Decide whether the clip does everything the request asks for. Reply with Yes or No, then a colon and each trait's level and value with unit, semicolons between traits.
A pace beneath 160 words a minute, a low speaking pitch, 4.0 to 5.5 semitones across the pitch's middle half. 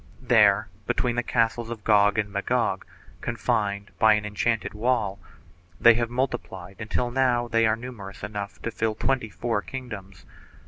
No: average, 150 wpm; low, 110 Hz; average, 2.7 semitones